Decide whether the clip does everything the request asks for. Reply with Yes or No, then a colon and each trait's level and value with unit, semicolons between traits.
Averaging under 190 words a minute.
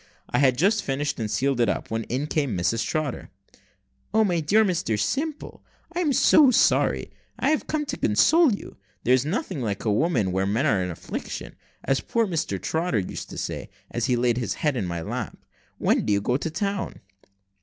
No: average, 195 wpm